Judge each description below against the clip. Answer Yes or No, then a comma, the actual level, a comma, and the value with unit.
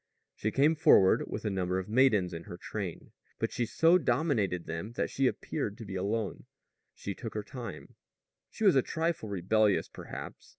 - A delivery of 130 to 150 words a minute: No, average, 180 wpm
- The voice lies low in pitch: Yes, low, 110 Hz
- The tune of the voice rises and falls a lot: Yes, wide, 5.9 semitones